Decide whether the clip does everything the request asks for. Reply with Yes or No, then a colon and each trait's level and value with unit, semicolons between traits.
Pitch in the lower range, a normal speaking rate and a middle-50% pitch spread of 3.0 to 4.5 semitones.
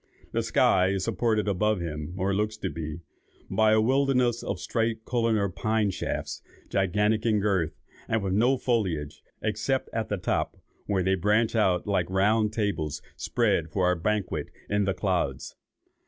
Yes: low, 105 Hz; average, 160 wpm; average, 3.3 semitones